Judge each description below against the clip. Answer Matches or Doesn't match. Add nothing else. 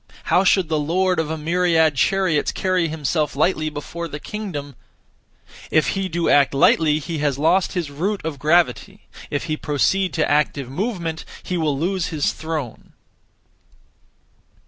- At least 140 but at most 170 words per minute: Matches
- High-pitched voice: Doesn't match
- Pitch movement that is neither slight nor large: Matches